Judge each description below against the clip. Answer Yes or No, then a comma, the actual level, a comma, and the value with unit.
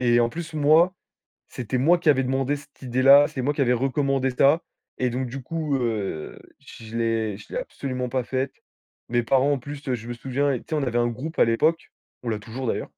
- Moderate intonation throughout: Yes, average, 3.1 semitones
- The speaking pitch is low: Yes, low, 130 Hz